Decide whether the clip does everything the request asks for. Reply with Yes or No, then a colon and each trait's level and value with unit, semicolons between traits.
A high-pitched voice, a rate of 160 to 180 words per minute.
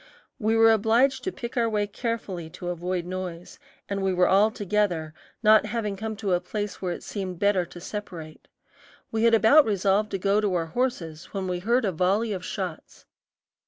No: high, 200 Hz; average, 195 wpm